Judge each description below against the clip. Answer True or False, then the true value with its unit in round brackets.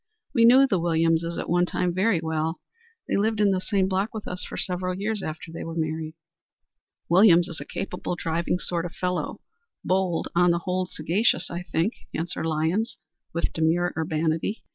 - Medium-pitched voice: True (175 Hz)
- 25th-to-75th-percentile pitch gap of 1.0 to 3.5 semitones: True (2.6 semitones)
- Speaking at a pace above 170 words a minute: True (185 wpm)